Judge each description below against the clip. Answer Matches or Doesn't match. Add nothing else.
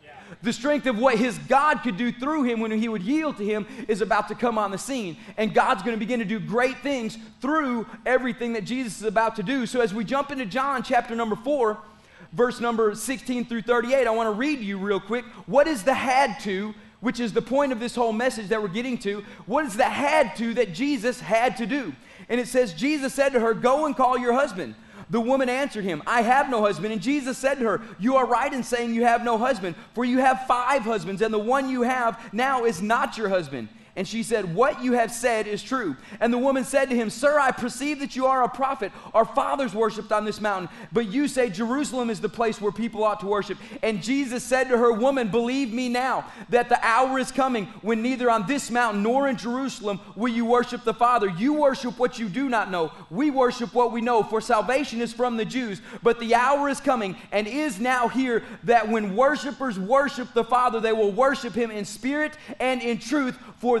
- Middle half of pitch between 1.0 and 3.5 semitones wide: Matches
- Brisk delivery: Matches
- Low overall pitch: Doesn't match